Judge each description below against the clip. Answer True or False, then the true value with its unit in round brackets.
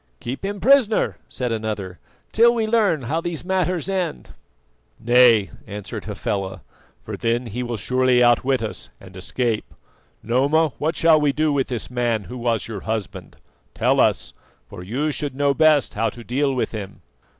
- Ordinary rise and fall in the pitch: False (5.7 semitones)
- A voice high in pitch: False (125 Hz)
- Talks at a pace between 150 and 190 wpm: True (165 wpm)